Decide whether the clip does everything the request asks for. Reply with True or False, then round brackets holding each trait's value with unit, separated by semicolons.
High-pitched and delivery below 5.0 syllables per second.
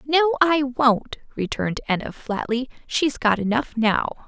True (255 Hz; 4.5 syllables/s)